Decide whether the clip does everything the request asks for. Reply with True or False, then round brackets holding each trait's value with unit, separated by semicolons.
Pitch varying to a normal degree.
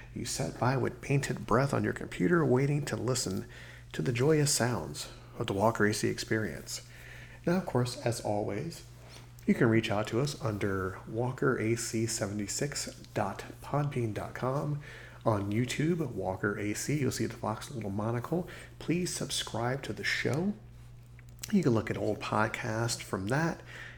True (3.7 semitones)